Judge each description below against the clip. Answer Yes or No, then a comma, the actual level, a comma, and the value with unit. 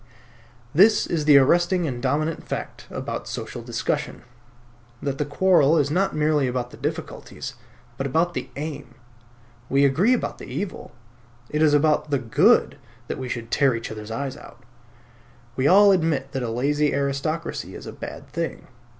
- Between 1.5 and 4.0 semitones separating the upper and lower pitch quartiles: Yes, average, 3.5 semitones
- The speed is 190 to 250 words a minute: No, average, 165 wpm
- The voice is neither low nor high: Yes, medium, 145 Hz